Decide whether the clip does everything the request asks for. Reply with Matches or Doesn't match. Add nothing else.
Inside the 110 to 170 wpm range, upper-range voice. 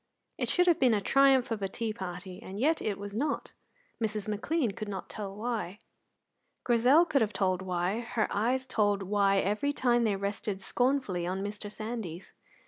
Doesn't match